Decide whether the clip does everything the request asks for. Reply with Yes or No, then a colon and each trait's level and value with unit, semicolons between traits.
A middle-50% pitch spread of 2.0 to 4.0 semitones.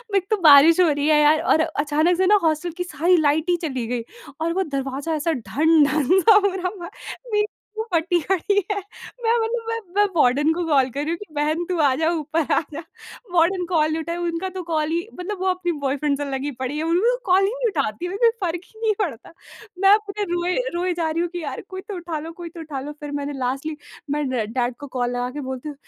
Yes: average, 3.7 semitones